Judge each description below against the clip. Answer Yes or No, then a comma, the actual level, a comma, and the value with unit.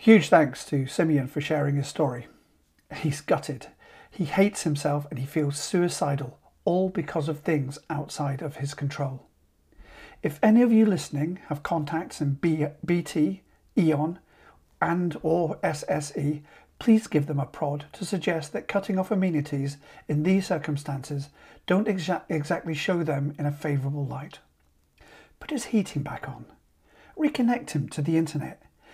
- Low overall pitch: No, medium, 155 Hz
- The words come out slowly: No, average, 145 wpm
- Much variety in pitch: No, average, 3.7 semitones